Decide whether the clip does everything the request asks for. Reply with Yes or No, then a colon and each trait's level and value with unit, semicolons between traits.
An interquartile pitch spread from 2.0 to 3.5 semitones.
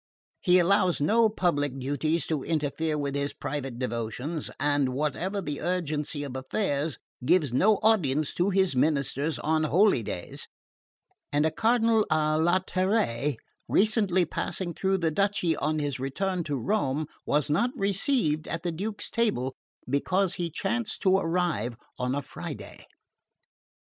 No: average, 5.1 semitones